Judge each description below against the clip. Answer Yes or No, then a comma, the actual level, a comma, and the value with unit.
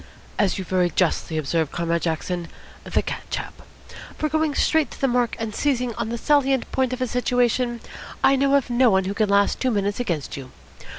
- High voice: Yes, high, 235 Hz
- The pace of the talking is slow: No, average, 200 wpm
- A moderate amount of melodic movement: No, wide, 5.8 semitones